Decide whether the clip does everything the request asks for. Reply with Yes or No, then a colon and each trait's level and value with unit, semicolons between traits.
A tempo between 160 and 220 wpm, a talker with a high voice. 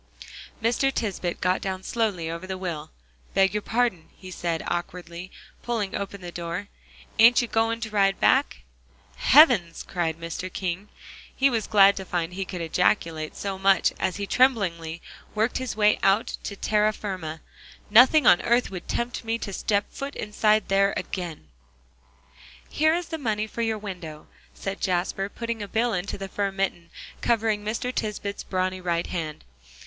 Yes: average, 165 wpm; high, 195 Hz